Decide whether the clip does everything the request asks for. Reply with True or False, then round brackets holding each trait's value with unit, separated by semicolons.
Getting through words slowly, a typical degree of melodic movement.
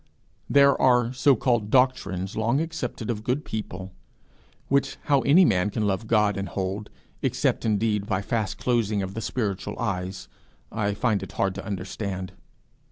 False (160 wpm; 4.0 semitones)